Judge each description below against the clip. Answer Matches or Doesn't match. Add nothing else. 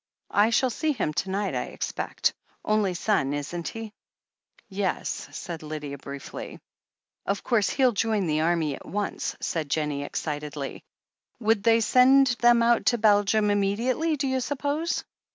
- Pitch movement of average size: Doesn't match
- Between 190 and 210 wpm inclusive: Doesn't match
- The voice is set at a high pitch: Matches